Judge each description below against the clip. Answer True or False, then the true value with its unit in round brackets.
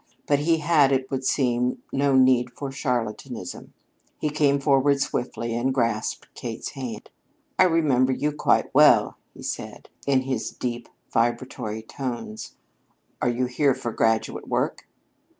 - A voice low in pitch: True (130 Hz)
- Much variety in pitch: False (2.7 semitones)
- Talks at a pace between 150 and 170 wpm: False (140 wpm)